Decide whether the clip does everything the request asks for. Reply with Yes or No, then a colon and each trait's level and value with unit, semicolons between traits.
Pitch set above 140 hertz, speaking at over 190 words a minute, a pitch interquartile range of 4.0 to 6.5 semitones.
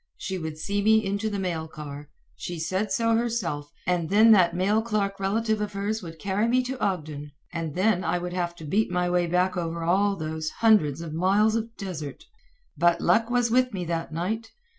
Yes: medium, 185 Hz; fast, 205 wpm; average, 4.5 semitones